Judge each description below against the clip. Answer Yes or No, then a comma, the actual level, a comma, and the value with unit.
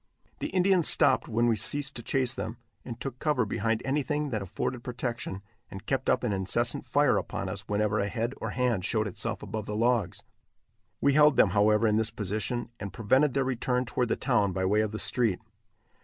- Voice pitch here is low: Yes, low, 120 Hz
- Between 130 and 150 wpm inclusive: No, average, 200 wpm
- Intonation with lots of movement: No, average, 3.6 semitones